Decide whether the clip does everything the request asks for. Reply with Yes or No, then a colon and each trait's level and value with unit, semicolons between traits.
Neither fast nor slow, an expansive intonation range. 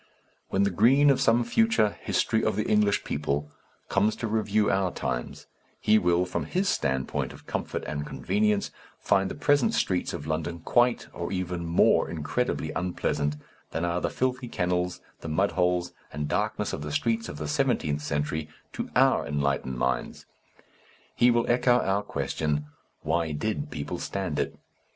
Yes: average, 160 wpm; wide, 6.2 semitones